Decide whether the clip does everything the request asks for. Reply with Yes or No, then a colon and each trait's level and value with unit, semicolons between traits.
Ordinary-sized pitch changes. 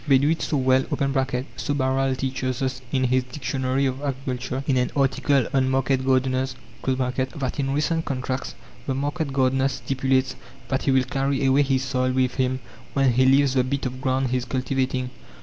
No: narrow, 1.0 semitones